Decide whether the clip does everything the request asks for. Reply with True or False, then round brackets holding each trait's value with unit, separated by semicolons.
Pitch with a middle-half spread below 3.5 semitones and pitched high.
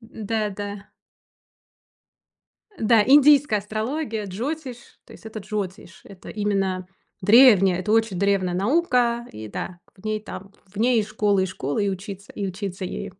True (2.9 semitones; 205 Hz)